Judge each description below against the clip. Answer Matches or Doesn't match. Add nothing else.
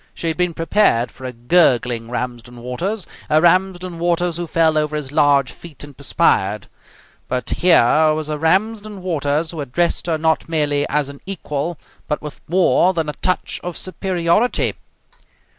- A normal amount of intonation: Matches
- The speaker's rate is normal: Matches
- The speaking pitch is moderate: Matches